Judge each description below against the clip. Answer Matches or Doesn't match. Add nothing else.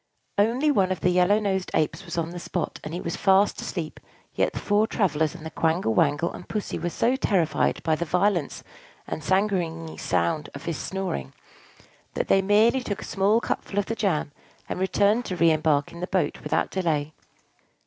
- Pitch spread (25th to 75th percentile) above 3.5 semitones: Matches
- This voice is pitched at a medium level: Matches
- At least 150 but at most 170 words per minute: Doesn't match